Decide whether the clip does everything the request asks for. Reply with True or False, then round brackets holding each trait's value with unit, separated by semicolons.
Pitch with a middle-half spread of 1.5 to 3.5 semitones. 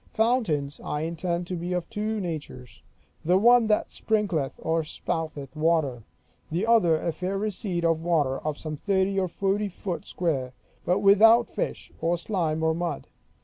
False (4.1 semitones)